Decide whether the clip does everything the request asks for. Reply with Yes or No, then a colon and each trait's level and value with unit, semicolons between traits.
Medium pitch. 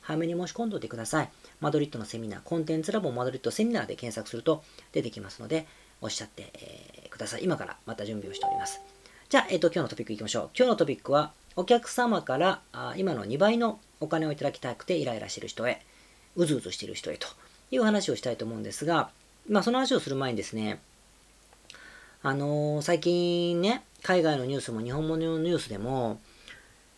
Yes: medium, 155 Hz